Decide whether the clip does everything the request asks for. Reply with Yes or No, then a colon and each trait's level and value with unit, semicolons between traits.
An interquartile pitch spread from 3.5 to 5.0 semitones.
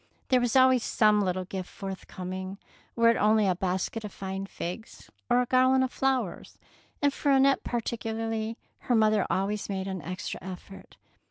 Yes: average, 4.3 semitones